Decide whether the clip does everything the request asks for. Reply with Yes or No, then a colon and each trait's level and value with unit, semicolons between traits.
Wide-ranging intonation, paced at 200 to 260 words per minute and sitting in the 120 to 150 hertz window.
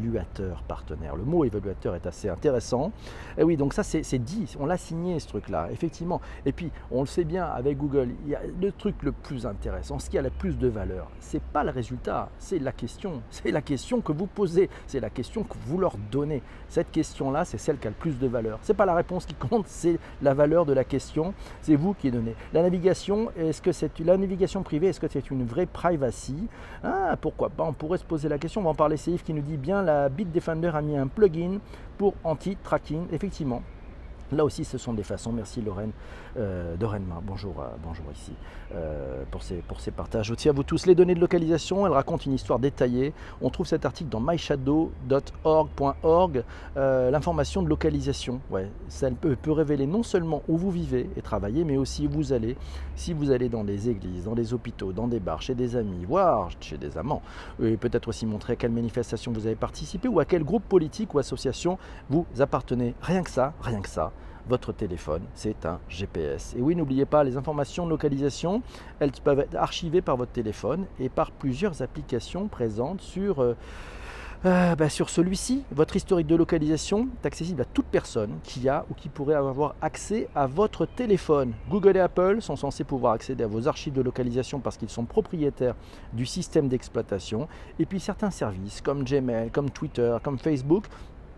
Yes: wide, 6.4 semitones; average, 210 wpm; medium, 140 Hz